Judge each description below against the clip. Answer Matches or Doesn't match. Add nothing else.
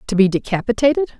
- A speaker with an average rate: Matches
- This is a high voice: Matches